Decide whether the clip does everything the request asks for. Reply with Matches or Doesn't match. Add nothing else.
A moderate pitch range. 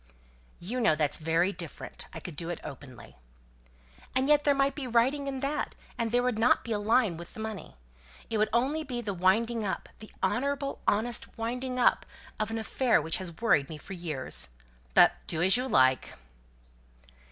Doesn't match